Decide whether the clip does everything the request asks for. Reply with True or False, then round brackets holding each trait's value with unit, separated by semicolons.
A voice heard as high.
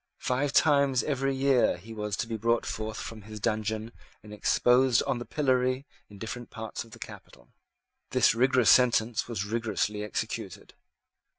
False (115 Hz)